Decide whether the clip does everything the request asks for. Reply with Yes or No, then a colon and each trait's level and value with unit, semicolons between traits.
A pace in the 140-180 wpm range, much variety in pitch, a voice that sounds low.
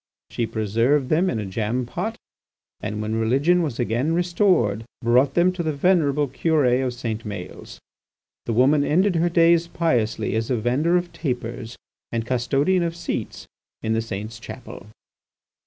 Yes: average, 155 wpm; wide, 6.6 semitones; low, 130 Hz